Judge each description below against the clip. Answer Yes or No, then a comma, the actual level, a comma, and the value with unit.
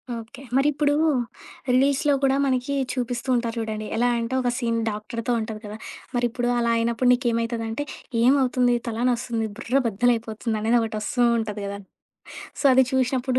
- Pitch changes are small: Yes, narrow, 2.1 semitones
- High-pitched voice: Yes, high, 240 Hz